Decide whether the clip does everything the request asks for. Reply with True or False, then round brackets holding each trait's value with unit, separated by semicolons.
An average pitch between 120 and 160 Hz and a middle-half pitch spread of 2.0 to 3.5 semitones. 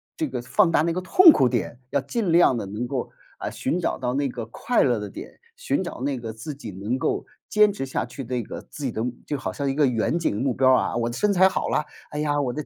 False (135 Hz; 4.5 semitones)